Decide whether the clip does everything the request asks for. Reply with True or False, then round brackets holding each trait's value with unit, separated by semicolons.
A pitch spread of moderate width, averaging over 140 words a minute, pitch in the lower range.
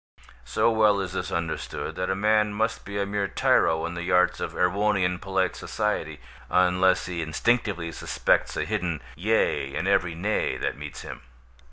True (3.0 semitones; 170 wpm; 90 Hz)